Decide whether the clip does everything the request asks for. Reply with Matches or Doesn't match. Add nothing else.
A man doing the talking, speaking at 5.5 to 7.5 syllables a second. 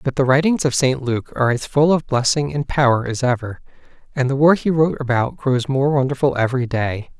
Matches